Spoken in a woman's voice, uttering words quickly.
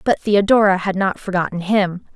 No: female; average, 165 wpm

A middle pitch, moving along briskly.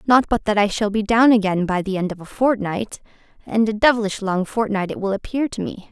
No: high, 210 Hz; fast, 245 wpm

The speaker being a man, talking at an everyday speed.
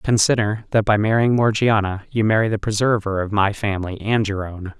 Yes: male; average, 190 wpm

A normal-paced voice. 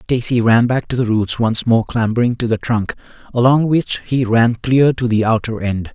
No: fast, 210 wpm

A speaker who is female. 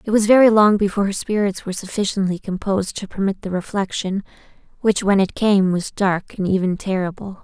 Yes: female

